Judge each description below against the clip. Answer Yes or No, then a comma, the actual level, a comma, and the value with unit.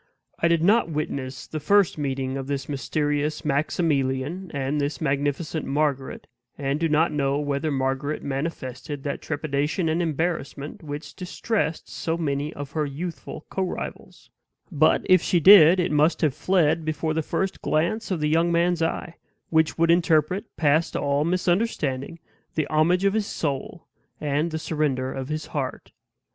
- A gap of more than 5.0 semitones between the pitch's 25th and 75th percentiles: No, average, 3.1 semitones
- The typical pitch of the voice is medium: Yes, medium, 155 Hz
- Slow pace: No, average, 155 wpm